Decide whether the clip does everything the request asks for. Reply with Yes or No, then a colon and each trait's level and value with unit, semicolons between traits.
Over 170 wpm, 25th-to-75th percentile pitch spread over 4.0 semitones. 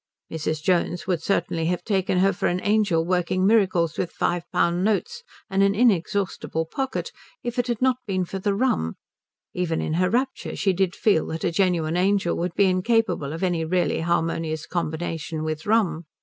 No: average, 180 wpm; average, 3.3 semitones